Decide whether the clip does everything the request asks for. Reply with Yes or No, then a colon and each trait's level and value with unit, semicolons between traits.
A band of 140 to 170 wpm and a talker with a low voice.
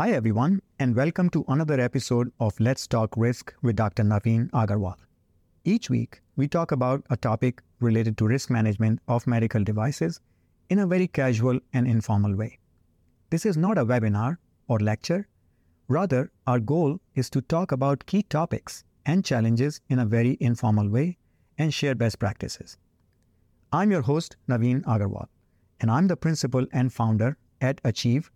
Yes: average, 160 wpm; low, 125 Hz